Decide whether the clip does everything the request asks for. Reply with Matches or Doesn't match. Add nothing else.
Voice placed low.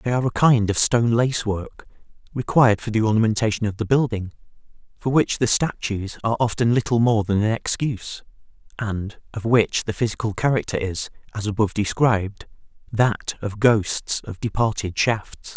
Matches